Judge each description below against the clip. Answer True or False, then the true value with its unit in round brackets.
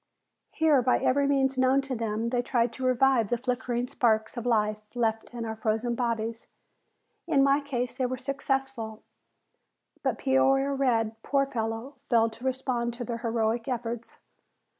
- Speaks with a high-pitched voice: True (245 Hz)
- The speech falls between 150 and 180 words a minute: True (160 wpm)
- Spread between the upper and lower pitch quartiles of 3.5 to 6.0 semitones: False (2.7 semitones)